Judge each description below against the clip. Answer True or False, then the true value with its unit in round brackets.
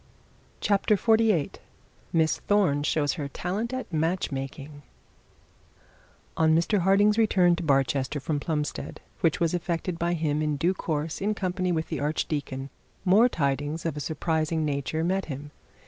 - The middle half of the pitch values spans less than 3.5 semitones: False (3.8 semitones)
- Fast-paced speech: False (145 wpm)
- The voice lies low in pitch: False (160 Hz)